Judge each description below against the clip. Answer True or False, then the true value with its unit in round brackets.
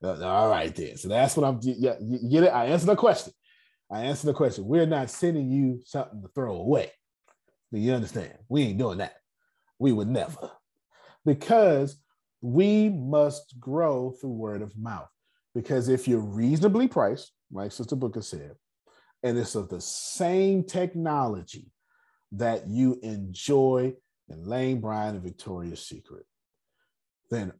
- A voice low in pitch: True (130 Hz)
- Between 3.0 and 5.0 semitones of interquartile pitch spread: False (5.6 semitones)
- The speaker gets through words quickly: False (150 wpm)